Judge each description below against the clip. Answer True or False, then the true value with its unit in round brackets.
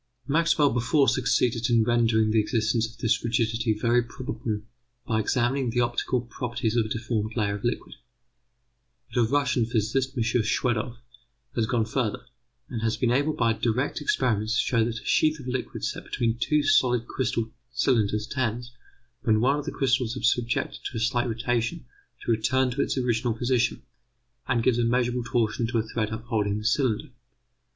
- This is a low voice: True (120 Hz)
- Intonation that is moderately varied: False (2.1 semitones)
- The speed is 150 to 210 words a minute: True (175 wpm)